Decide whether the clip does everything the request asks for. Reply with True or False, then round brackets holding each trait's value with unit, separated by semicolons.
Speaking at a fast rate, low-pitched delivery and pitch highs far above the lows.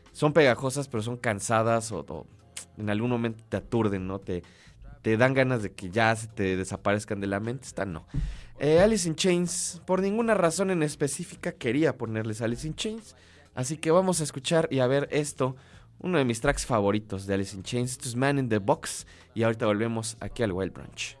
True (205 wpm; 120 Hz; 6.0 semitones)